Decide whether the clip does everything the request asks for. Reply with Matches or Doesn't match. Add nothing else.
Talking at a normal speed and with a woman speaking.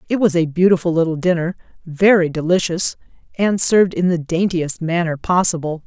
Matches